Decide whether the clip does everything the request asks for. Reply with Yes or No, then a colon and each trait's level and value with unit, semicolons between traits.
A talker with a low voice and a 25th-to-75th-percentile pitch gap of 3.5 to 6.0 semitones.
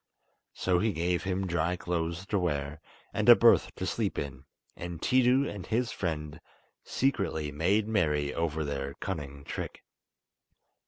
Yes: very low, 85 Hz; average, 4.5 semitones